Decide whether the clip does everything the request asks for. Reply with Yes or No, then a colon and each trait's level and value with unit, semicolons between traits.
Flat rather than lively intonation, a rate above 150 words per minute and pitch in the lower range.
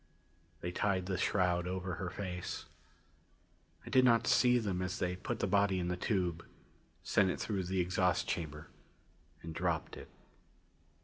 Yes: narrow, 1.9 semitones; average, 160 wpm; very low, 90 Hz